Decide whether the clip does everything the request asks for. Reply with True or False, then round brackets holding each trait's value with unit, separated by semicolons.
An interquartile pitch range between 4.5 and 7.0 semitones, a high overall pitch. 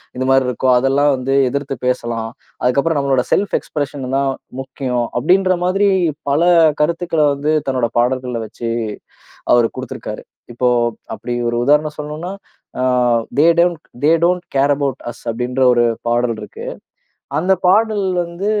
False (4.8 semitones; 140 Hz)